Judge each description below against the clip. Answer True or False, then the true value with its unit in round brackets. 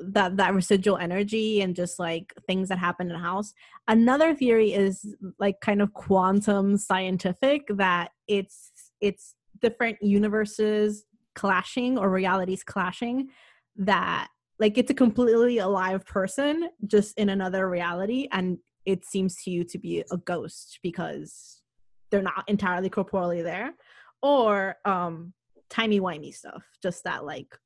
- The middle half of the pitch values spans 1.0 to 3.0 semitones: True (2.7 semitones)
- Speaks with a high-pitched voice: True (195 Hz)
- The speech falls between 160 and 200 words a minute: False (140 wpm)